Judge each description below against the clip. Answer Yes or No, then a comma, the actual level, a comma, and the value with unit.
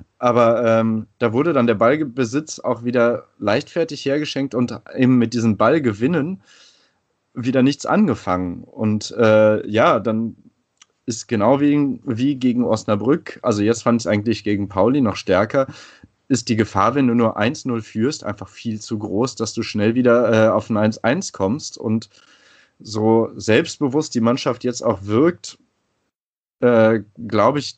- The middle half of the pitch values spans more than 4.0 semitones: No, average, 2.8 semitones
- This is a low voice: Yes, low, 115 Hz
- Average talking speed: Yes, average, 155 wpm